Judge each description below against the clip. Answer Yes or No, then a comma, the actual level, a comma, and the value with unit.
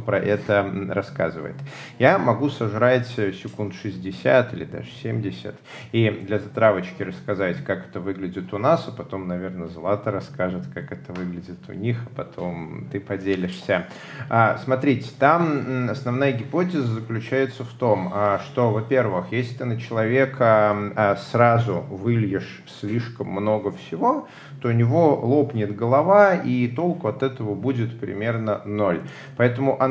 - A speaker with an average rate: Yes, average, 130 wpm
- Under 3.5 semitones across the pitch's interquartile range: No, average, 4.4 semitones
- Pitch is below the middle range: Yes, low, 115 Hz